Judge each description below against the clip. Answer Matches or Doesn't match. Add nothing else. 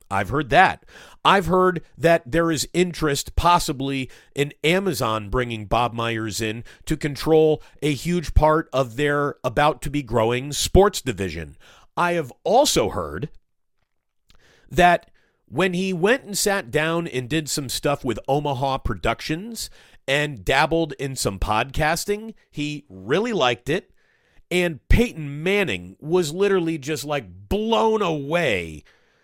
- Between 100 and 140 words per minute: Matches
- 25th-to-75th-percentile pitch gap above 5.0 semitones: Matches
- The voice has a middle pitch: Matches